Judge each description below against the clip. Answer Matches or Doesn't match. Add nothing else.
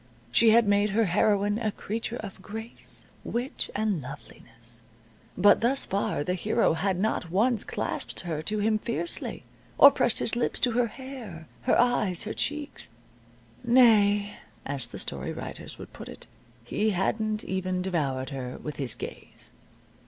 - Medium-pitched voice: Doesn't match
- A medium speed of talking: Matches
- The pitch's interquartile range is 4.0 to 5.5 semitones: Matches